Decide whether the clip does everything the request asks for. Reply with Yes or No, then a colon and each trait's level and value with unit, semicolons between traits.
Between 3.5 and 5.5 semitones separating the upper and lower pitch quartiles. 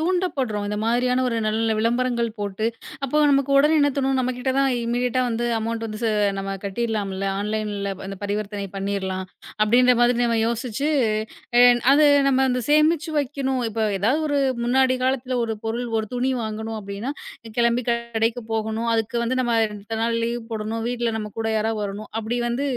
No: average, 2.8 semitones